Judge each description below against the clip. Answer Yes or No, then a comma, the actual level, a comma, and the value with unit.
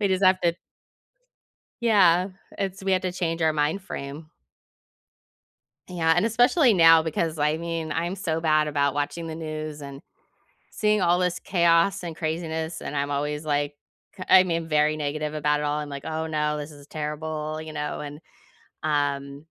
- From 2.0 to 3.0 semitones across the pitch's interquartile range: Yes, narrow, 2.6 semitones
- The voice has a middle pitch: Yes, medium, 160 Hz